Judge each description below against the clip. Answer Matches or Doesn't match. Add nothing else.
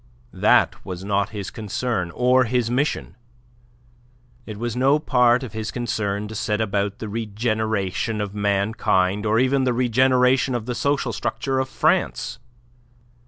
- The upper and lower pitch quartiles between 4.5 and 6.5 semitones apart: Doesn't match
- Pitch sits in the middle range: Doesn't match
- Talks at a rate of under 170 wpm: Matches